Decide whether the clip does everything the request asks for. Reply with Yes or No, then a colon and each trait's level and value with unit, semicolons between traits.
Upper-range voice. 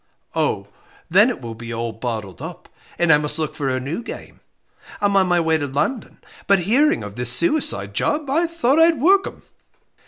No: medium, 165 Hz